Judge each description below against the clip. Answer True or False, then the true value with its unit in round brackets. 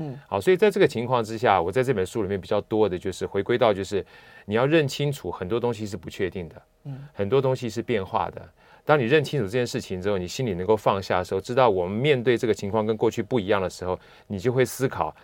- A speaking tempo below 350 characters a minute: False (375 characters per minute)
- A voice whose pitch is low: True (115 Hz)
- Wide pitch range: False (4.6 semitones)